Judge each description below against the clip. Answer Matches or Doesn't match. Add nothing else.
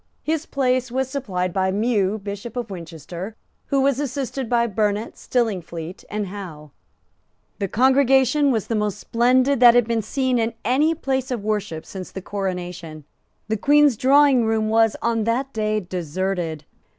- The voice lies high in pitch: Matches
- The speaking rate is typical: Matches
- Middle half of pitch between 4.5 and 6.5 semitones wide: Matches